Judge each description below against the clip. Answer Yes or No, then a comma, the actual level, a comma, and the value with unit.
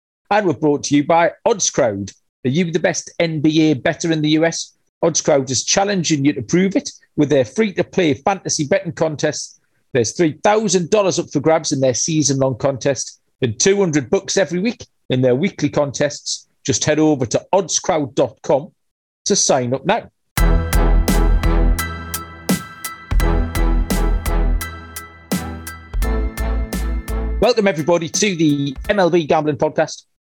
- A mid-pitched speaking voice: Yes, medium, 150 Hz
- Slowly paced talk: Yes, slow, 130 wpm